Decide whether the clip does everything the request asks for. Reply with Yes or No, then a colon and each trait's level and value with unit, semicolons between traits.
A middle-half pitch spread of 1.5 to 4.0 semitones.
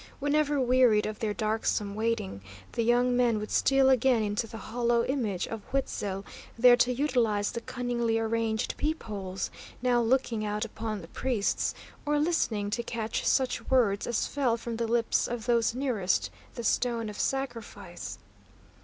Yes: narrow, 2.6 semitones